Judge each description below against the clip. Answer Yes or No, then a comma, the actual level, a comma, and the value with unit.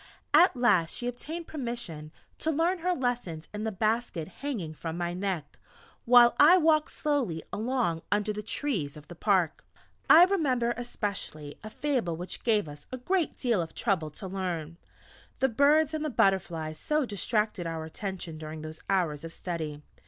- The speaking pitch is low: No, high, 205 Hz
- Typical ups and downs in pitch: No, wide, 7.8 semitones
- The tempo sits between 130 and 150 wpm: No, average, 165 wpm